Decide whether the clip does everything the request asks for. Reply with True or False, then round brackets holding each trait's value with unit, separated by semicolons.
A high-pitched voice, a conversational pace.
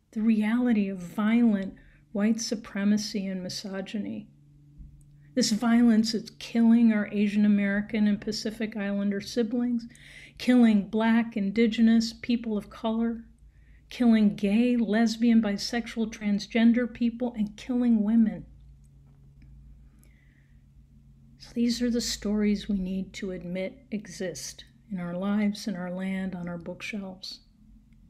False (210 Hz; 115 wpm)